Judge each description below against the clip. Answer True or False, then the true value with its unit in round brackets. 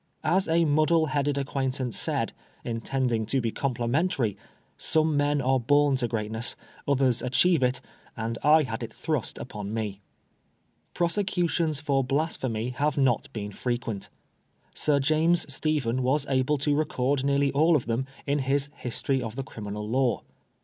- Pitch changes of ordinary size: True (3.8 semitones)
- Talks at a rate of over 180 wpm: False (150 wpm)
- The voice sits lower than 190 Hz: True (135 Hz)